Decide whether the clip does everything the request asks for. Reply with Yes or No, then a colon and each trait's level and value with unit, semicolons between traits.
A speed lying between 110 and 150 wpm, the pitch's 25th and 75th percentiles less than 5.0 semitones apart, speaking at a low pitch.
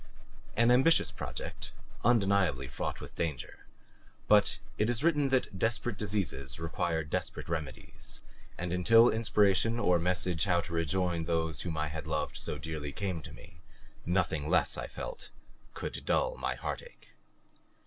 No: average, 145 wpm; wide, 5.6 semitones; very low, 90 Hz